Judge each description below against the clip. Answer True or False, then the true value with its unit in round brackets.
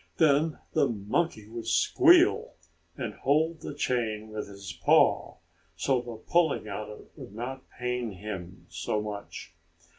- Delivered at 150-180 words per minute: False (140 wpm)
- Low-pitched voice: True (110 Hz)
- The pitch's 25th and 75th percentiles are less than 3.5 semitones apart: False (4.4 semitones)